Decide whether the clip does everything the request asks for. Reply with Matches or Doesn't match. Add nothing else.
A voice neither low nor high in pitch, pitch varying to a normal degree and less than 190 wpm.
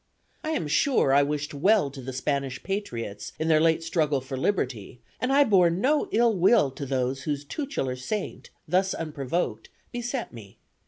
Doesn't match